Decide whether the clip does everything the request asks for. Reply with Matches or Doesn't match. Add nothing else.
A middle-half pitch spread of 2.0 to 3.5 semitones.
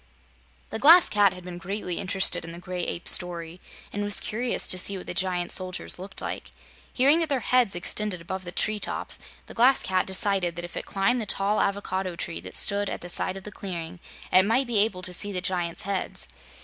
Matches